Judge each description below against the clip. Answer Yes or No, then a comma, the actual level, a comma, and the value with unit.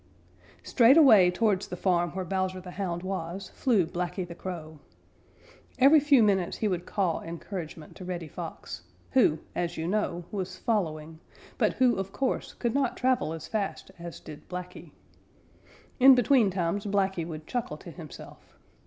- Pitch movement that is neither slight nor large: Yes, average, 3.9 semitones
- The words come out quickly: No, average, 160 wpm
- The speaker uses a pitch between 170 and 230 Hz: Yes, medium, 185 Hz